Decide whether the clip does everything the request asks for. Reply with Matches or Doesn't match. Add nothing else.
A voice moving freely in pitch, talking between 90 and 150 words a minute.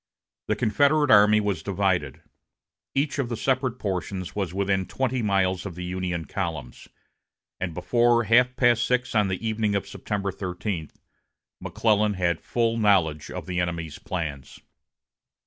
Doesn't match